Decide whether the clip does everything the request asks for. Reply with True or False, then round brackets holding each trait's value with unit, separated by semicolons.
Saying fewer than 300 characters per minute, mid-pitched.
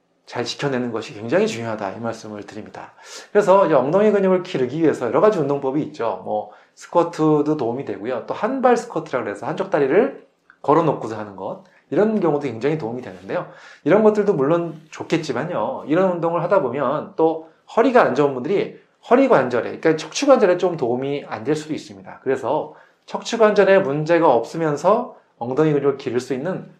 False (400 characters per minute; 160 Hz)